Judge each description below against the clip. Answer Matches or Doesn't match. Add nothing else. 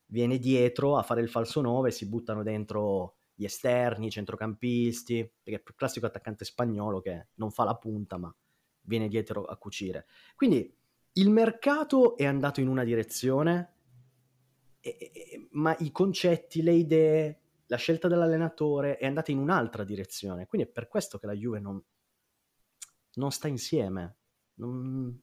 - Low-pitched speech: Matches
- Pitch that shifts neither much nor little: Doesn't match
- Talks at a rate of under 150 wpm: Doesn't match